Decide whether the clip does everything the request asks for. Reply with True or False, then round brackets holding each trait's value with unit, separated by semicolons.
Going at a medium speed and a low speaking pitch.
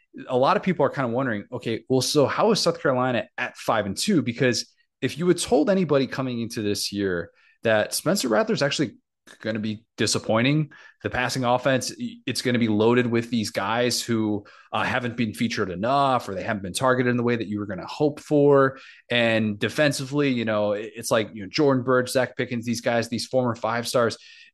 False (215 wpm; 125 Hz)